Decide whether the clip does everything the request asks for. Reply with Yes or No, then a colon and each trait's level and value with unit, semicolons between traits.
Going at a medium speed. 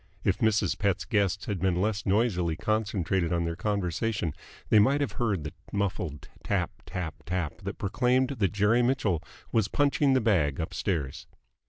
Yes: average, 160 wpm